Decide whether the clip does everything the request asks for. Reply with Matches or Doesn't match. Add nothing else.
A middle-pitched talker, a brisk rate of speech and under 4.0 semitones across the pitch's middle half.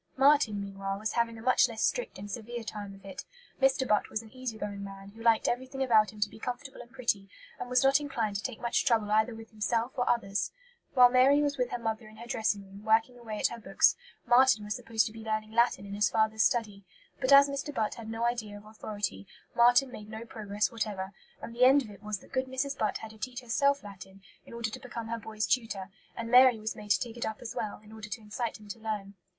Doesn't match